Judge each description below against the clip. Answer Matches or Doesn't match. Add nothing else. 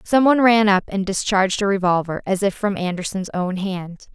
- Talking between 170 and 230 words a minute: Matches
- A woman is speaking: Matches